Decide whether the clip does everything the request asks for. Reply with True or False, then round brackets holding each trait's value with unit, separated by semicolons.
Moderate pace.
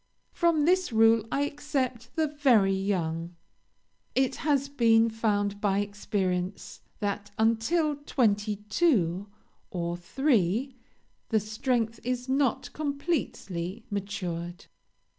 False (105 wpm)